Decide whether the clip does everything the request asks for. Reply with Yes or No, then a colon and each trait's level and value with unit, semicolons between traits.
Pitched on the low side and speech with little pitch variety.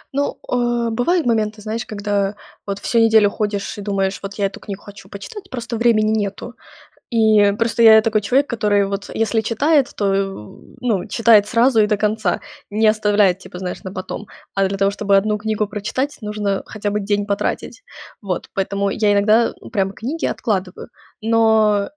No: high, 210 Hz; narrow, 2.2 semitones